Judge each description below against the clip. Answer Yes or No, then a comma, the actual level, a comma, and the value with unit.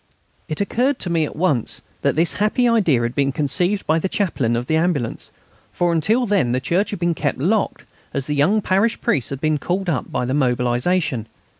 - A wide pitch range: Yes, wide, 6.1 semitones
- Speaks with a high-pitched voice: No, medium, 160 Hz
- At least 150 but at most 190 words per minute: No, fast, 205 wpm